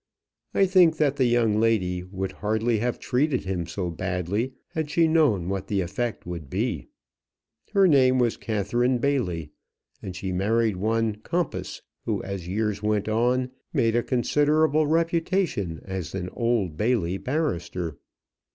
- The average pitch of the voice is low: Yes, low, 110 Hz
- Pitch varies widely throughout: Yes, wide, 5.7 semitones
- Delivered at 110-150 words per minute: Yes, average, 145 wpm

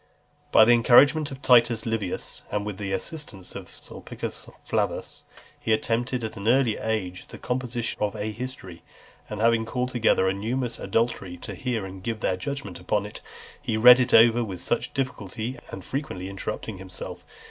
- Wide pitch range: No, average, 3.9 semitones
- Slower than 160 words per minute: No, average, 175 wpm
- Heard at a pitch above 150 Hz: No, low, 110 Hz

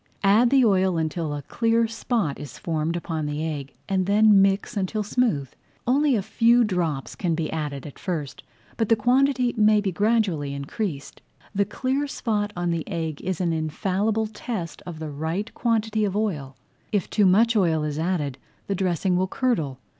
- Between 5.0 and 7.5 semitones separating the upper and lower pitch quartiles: Yes, wide, 5.5 semitones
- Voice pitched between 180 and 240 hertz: Yes, high, 190 Hz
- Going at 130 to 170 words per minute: No, average, 185 wpm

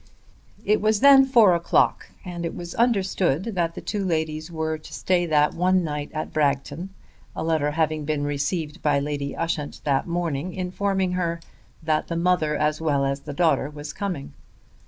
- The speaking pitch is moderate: Yes, medium, 165 Hz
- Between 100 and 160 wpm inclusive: No, average, 175 wpm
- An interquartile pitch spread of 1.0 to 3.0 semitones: No, average, 3.5 semitones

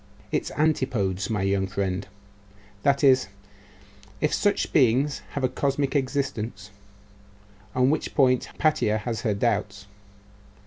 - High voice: No, low, 125 Hz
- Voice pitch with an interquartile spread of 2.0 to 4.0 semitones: No, wide, 5.6 semitones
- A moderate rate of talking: No, slow, 120 wpm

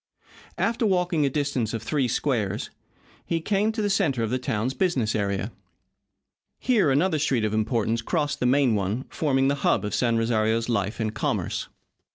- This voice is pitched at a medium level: No, low, 130 Hz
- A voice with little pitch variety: No, wide, 5.6 semitones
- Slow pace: No, average, 175 wpm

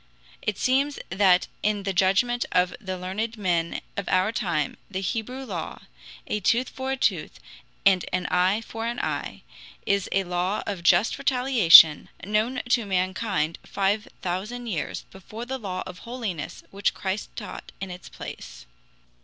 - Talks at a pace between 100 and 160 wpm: Yes, average, 155 wpm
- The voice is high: Yes, high, 195 Hz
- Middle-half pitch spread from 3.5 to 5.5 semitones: Yes, average, 4.0 semitones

